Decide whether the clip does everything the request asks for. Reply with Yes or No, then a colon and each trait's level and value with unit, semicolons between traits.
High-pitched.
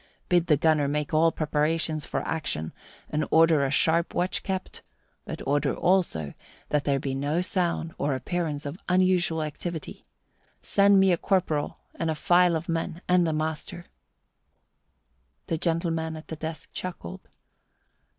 No: medium, 160 Hz